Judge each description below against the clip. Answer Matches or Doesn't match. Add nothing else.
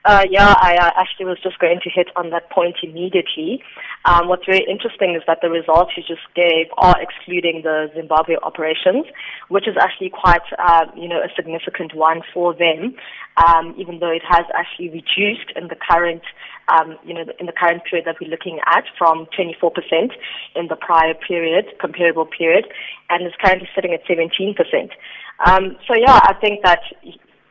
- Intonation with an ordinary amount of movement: Doesn't match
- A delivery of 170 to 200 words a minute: Matches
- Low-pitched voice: Doesn't match